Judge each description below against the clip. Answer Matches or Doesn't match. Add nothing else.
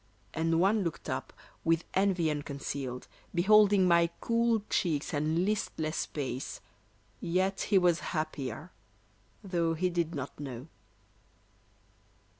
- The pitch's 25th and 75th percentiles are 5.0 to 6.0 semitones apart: Doesn't match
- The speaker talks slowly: Matches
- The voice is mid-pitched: Matches